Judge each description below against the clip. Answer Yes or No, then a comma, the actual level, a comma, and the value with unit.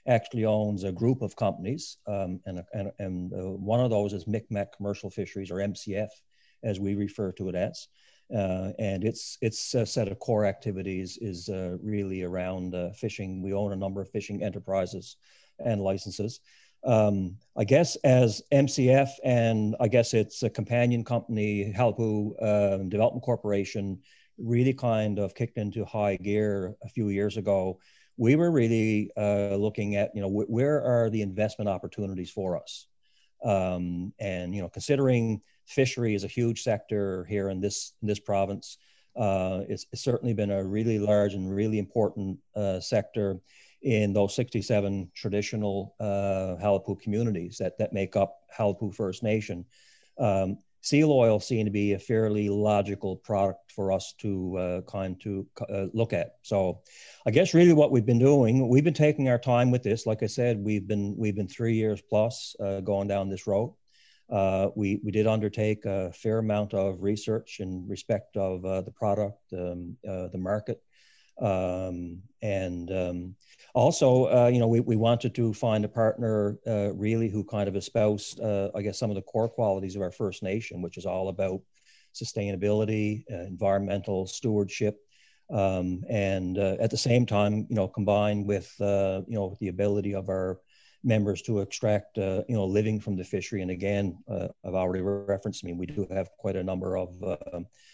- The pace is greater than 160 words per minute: Yes, average, 175 wpm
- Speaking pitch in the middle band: No, low, 105 Hz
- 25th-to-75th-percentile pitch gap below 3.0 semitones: Yes, narrow, 2.5 semitones